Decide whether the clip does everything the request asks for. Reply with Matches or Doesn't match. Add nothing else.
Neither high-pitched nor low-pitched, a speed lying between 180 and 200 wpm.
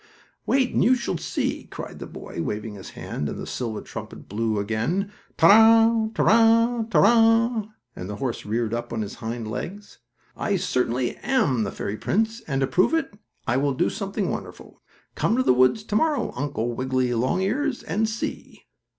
Matches